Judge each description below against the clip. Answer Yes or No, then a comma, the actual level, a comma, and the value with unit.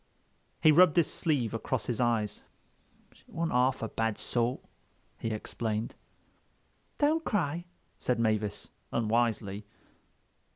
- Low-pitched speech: Yes, low, 120 Hz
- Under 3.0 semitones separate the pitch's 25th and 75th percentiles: No, average, 5.2 semitones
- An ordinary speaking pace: No, slow, 115 wpm